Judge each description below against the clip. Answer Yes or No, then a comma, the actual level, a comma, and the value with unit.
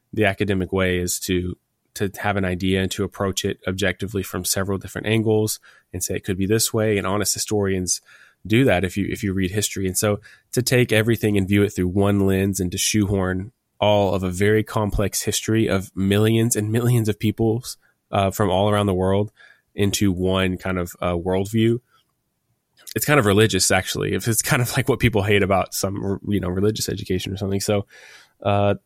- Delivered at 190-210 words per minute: Yes, average, 200 wpm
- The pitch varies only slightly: Yes, narrow, 2.2 semitones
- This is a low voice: Yes, low, 100 Hz